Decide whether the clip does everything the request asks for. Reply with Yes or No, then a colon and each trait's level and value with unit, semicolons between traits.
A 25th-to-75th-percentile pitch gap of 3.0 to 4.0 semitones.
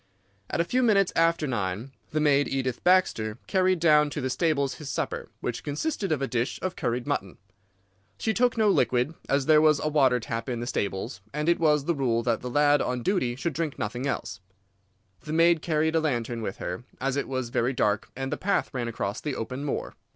No: average, 4.7 semitones